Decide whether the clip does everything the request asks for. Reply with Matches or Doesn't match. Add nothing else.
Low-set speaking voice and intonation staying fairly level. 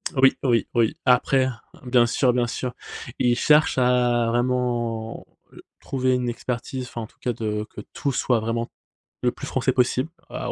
Matches